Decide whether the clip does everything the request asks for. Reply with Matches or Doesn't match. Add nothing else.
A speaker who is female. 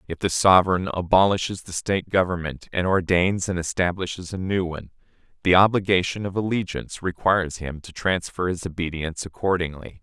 Doesn't match